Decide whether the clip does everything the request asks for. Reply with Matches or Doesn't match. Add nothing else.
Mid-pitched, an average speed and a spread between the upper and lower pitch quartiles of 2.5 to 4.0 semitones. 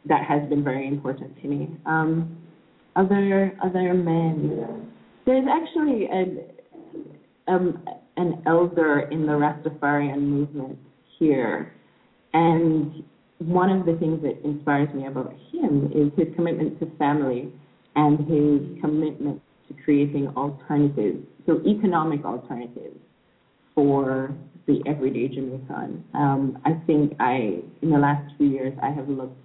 Doesn't match